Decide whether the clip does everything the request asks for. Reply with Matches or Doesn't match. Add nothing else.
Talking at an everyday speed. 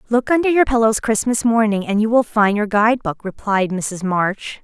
Matches